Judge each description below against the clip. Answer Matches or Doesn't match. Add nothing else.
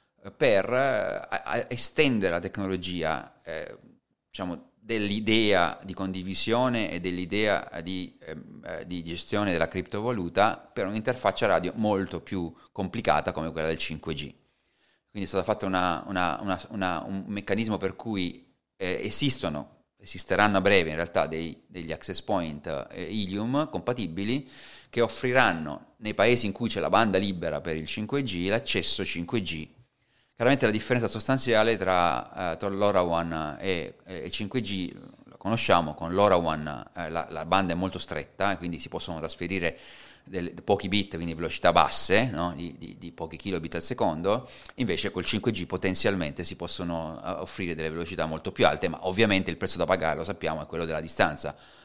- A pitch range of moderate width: Matches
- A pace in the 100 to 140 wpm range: Doesn't match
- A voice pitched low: Matches